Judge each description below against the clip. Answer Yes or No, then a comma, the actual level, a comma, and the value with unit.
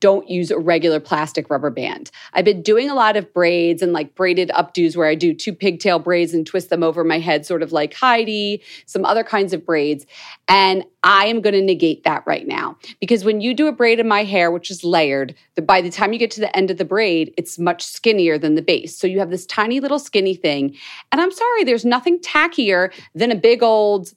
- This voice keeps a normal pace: No, fast, 235 wpm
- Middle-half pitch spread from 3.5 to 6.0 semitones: Yes, average, 4.3 semitones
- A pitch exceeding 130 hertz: Yes, high, 190 Hz